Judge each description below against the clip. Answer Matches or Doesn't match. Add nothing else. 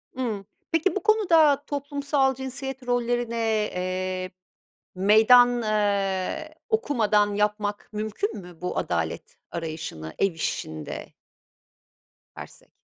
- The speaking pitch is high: Matches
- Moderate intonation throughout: Doesn't match